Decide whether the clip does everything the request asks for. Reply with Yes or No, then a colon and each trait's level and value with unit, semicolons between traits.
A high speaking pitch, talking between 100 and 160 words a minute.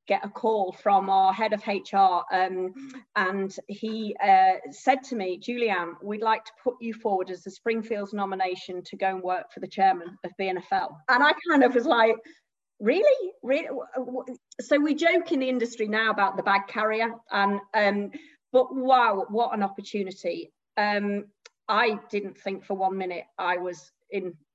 No: high, 205 Hz; average, 175 wpm